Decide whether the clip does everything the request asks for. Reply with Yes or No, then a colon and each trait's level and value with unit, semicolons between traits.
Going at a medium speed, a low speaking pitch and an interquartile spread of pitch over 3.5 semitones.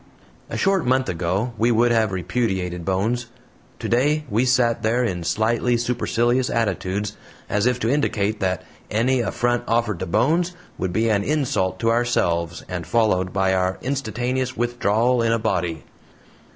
Yes: average, 150 wpm; low, 115 Hz; average, 4.5 semitones